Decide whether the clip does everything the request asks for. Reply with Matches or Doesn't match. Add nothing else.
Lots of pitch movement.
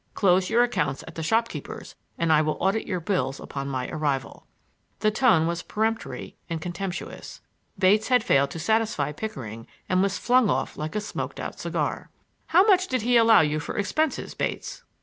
Matches